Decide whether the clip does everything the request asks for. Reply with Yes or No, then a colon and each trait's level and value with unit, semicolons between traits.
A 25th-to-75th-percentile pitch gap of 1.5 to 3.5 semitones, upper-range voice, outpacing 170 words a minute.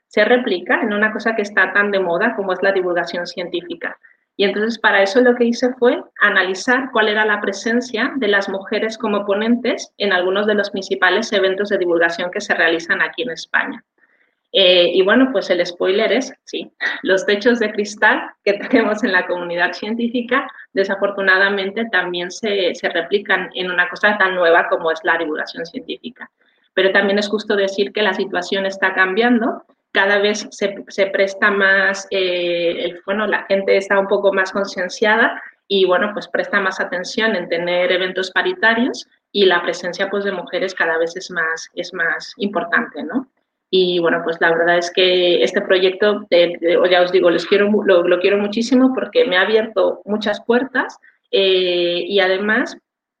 Yes: average, 3.0 semitones; high, 195 Hz; average, 180 wpm